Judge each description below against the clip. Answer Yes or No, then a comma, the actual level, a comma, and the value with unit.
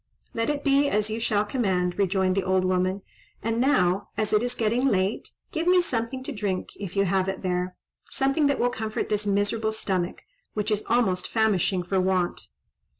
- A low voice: No, high, 205 Hz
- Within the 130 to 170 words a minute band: No, average, 185 wpm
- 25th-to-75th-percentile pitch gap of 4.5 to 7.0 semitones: No, average, 3.8 semitones